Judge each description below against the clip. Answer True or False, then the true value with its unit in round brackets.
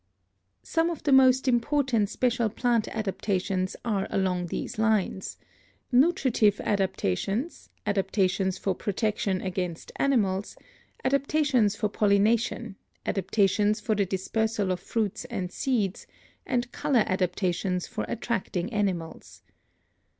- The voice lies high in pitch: True (210 Hz)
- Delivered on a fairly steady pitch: False (4.1 semitones)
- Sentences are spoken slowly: True (105 wpm)